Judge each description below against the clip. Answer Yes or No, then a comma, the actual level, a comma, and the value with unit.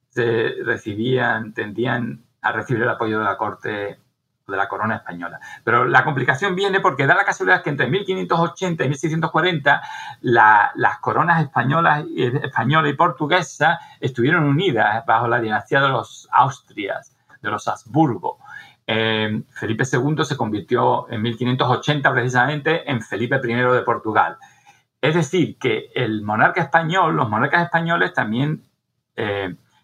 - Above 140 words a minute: No, average, 135 wpm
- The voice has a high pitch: No, medium, 140 Hz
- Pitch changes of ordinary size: No, wide, 5.9 semitones